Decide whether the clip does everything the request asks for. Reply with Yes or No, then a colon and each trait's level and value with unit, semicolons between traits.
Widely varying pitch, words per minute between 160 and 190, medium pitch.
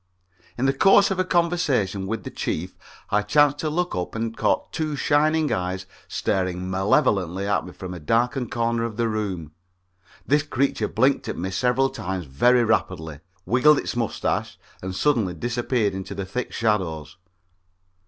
No: wide, 6.3 semitones; average, 165 wpm; low, 115 Hz